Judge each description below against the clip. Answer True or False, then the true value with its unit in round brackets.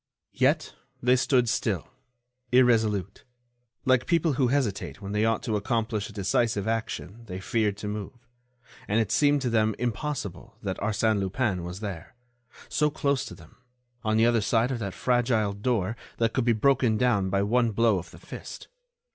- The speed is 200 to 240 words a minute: False (170 wpm)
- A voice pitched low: True (110 Hz)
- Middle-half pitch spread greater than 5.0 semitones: False (3.4 semitones)